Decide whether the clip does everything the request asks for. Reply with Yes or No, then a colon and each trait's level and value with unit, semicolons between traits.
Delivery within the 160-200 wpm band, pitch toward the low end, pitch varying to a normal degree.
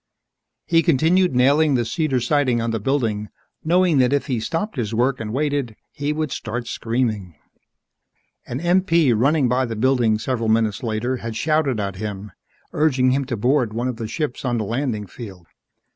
Yes: average, 180 wpm; low, 125 Hz; average, 4.3 semitones